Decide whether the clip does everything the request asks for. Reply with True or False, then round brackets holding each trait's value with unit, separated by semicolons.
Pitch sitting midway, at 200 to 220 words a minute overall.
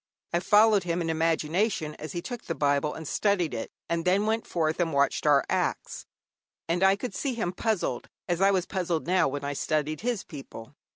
True (170 Hz; 205 wpm)